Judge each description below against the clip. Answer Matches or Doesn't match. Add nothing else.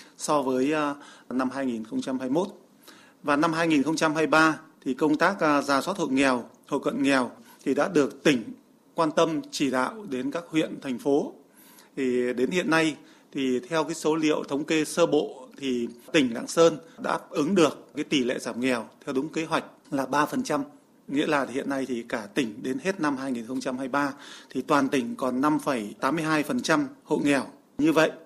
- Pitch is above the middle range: Doesn't match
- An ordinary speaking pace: Matches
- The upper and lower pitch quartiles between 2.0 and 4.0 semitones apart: Matches